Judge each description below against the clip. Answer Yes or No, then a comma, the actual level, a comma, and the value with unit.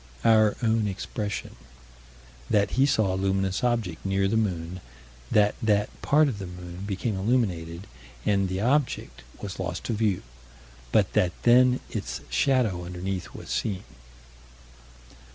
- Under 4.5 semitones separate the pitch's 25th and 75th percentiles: Yes, average, 3.4 semitones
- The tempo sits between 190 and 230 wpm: No, slow, 135 wpm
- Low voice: Yes, low, 100 Hz